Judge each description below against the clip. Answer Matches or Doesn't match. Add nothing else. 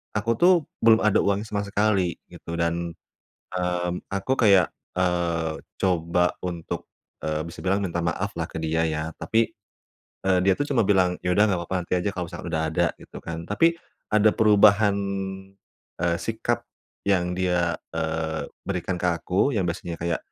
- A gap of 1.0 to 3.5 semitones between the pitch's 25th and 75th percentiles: Matches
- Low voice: Matches